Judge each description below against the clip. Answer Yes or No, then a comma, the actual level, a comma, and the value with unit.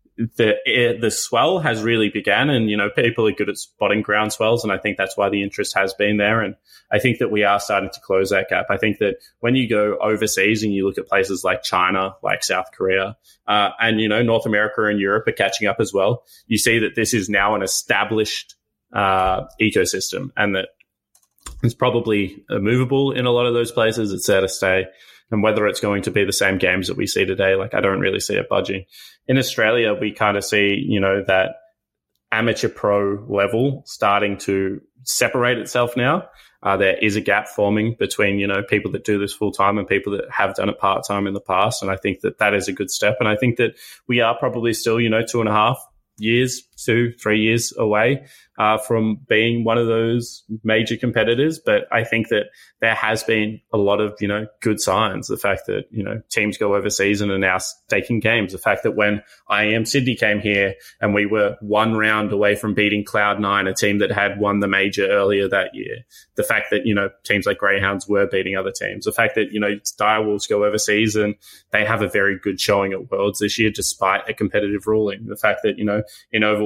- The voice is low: Yes, low, 105 Hz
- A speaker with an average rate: No, fast, 225 wpm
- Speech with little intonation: Yes, narrow, 2.1 semitones